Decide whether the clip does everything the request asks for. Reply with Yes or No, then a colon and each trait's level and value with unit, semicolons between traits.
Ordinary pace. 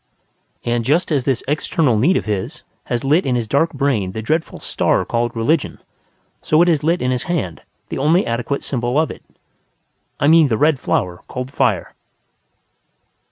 Yes: average, 175 wpm